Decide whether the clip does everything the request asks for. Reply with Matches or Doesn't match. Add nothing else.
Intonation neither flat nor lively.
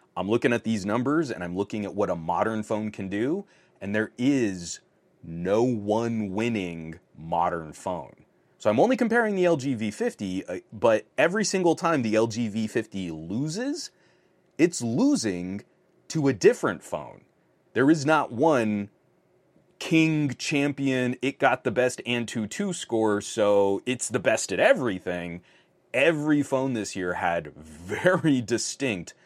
Doesn't match